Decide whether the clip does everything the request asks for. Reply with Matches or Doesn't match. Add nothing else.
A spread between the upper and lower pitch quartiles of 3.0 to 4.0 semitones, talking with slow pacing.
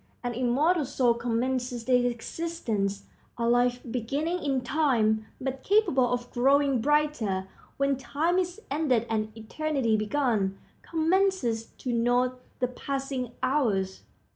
Matches